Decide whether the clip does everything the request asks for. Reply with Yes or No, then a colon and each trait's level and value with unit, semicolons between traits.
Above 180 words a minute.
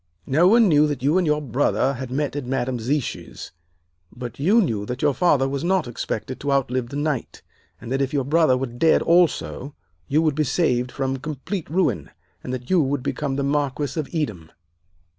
Yes: average, 200 wpm